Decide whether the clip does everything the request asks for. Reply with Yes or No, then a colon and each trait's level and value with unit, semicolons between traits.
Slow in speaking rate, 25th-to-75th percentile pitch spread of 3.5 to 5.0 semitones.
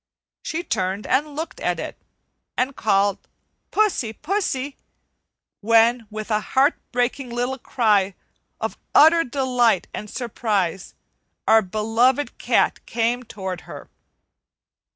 Yes: slow, 110 wpm; average, 3.9 semitones